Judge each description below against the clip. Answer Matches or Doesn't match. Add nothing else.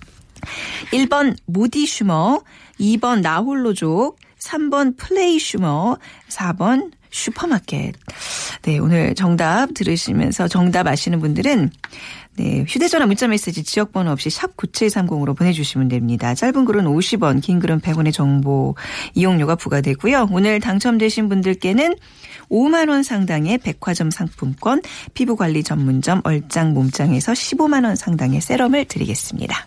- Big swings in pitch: Matches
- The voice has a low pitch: Doesn't match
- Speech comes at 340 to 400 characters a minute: Doesn't match